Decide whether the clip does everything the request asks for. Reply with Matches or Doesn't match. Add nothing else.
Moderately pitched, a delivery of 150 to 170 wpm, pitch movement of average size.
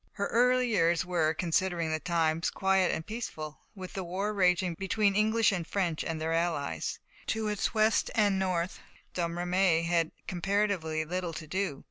Matches